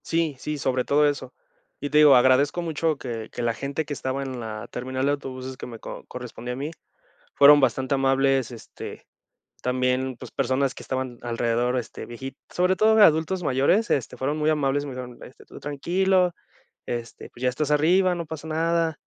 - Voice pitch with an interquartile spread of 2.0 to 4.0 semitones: Yes, average, 3.3 semitones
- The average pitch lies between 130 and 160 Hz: Yes, low, 135 Hz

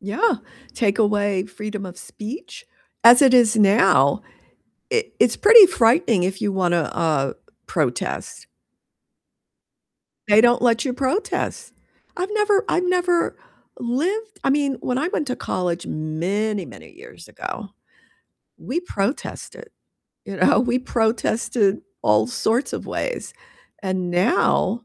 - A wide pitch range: Yes, wide, 6.8 semitones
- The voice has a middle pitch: No, high, 230 Hz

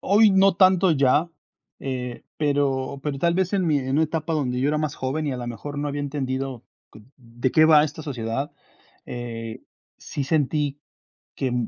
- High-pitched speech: No, medium, 145 Hz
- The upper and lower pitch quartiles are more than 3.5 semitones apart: No, average, 3.2 semitones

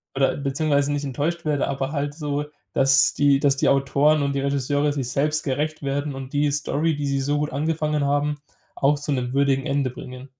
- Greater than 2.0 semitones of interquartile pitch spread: No, narrow, 1.3 semitones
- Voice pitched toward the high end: No, medium, 140 Hz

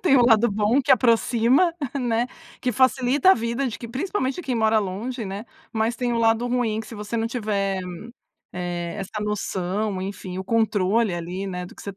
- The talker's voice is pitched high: Yes, high, 225 Hz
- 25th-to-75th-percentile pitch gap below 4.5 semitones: Yes, average, 3.6 semitones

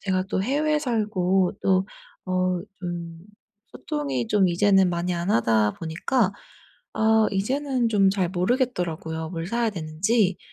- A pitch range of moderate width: Yes, average, 4.2 semitones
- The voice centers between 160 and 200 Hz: Yes, medium, 185 Hz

